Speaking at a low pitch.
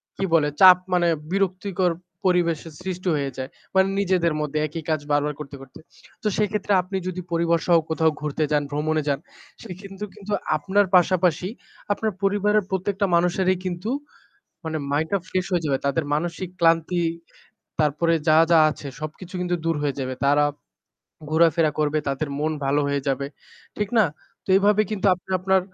No: medium, 170 Hz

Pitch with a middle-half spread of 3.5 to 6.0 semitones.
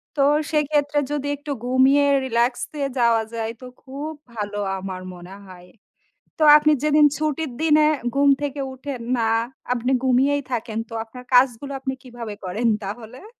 Yes: average, 4.1 semitones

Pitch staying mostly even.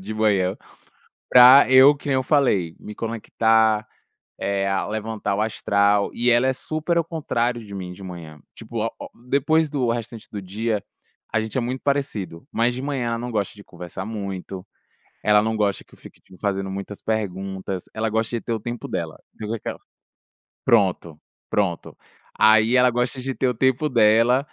No: average, 3.8 semitones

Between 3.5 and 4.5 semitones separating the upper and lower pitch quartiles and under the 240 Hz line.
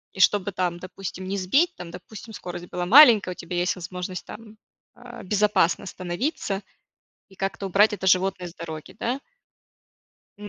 No: average, 2.8 semitones; high, 190 Hz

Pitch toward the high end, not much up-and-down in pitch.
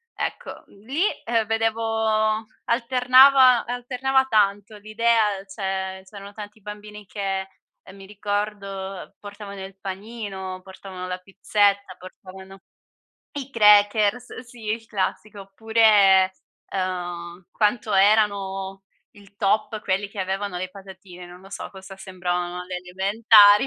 Yes: high, 200 Hz; narrow, 2.3 semitones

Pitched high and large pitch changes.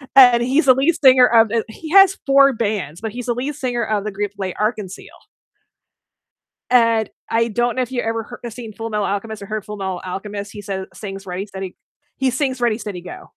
No: high, 225 Hz; average, 3.6 semitones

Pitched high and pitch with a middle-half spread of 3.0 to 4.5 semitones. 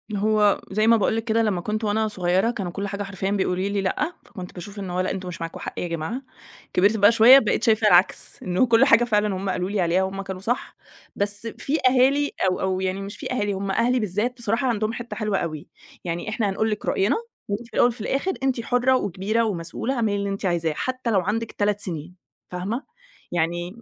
Yes: high, 205 Hz; average, 3.4 semitones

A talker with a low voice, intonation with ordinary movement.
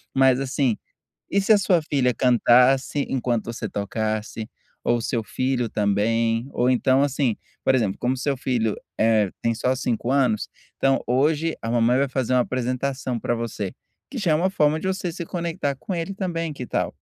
Yes: low, 130 Hz; average, 3.8 semitones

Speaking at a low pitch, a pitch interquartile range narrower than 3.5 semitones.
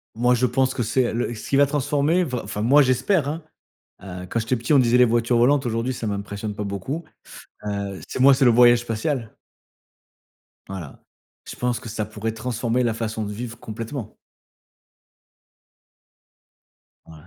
Yes: low, 120 Hz; average, 3.0 semitones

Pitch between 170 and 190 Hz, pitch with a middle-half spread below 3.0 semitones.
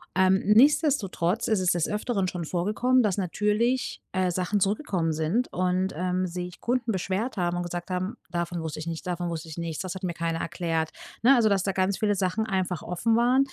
No: medium, 185 Hz; average, 3.4 semitones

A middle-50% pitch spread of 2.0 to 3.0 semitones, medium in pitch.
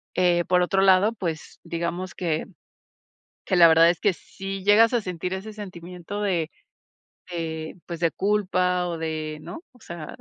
Yes: narrow, 2.5 semitones; medium, 180 Hz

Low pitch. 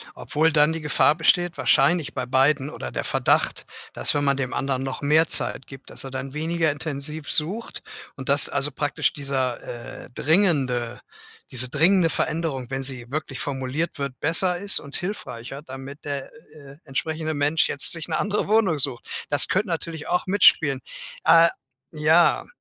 No: medium, 145 Hz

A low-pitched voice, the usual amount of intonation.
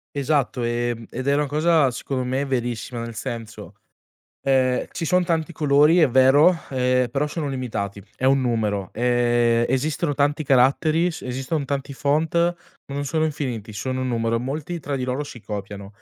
Yes: low, 130 Hz; average, 3.6 semitones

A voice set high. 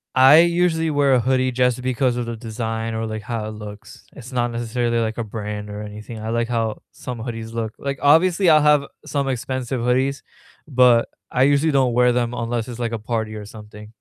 No: low, 120 Hz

